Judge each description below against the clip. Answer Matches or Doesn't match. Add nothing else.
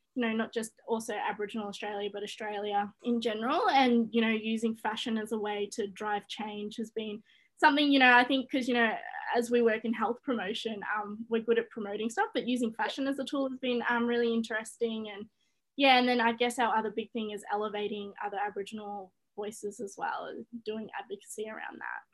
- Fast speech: Matches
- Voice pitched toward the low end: Doesn't match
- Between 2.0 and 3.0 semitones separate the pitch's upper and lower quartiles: Matches